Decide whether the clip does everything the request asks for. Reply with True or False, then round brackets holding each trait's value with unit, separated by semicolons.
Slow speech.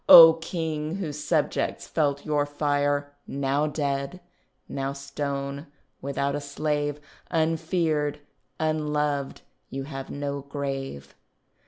True (105 wpm)